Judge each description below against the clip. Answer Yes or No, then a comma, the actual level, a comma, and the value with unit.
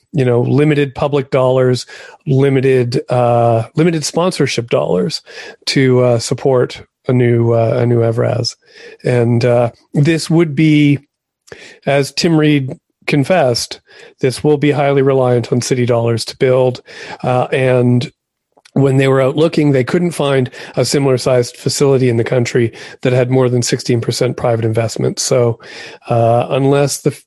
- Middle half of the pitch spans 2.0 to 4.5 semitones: Yes, average, 2.9 semitones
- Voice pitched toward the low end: Yes, low, 130 Hz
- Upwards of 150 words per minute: No, average, 145 wpm